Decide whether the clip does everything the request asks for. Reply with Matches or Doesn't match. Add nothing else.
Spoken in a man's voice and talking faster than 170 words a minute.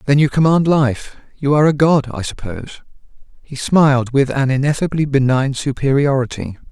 Doesn't match